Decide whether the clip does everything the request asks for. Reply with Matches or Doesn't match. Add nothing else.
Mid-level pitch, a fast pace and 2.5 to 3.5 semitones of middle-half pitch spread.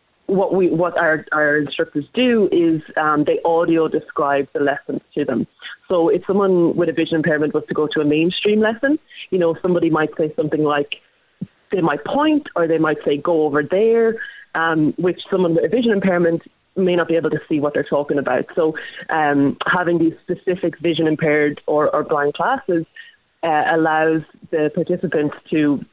Doesn't match